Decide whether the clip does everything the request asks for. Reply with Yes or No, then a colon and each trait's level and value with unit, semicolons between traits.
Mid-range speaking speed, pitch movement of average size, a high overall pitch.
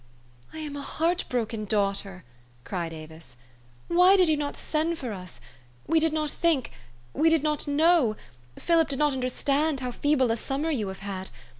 No: average, 175 wpm; wide, 7.3 semitones; very high, 280 Hz